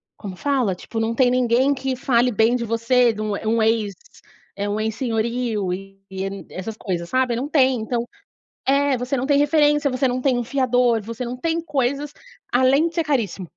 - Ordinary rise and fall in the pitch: Yes, average, 3.3 semitones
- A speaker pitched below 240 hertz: No, high, 245 Hz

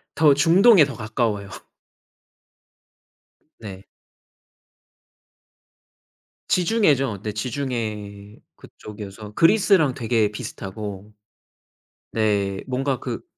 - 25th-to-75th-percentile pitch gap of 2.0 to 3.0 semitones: No, wide, 5.4 semitones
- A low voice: Yes, low, 110 Hz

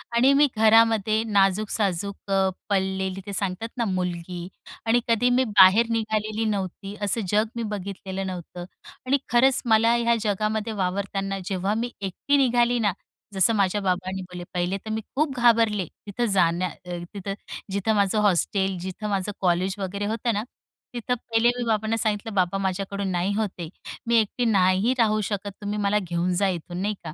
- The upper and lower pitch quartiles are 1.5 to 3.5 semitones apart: Yes, average, 2.9 semitones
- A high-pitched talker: Yes, high, 200 Hz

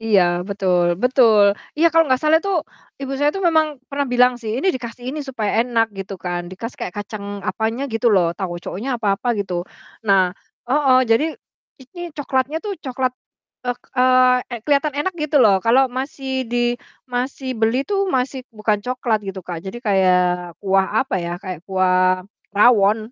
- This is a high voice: Yes, high, 245 Hz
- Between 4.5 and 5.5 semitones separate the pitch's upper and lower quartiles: Yes, average, 5.0 semitones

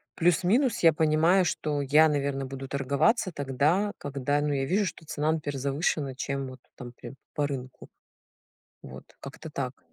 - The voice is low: No, medium, 145 Hz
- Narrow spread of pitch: No, average, 3.0 semitones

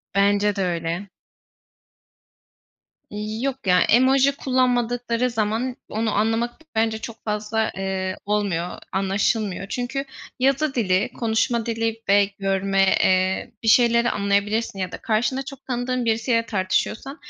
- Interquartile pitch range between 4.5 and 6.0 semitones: No, average, 3.4 semitones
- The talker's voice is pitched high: Yes, high, 220 Hz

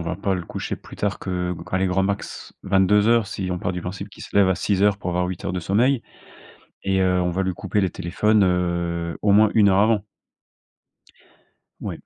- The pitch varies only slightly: Yes, narrow, 2.2 semitones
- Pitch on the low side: Yes, very low, 95 Hz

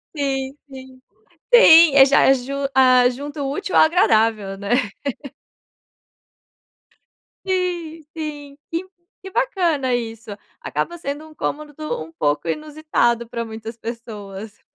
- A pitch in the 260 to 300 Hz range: Yes, very high, 270 Hz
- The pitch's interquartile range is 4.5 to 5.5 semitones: Yes, average, 5.2 semitones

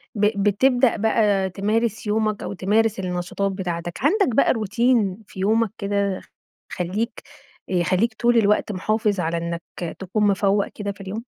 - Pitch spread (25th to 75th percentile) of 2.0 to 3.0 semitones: Yes, average, 2.7 semitones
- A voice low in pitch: No, high, 205 Hz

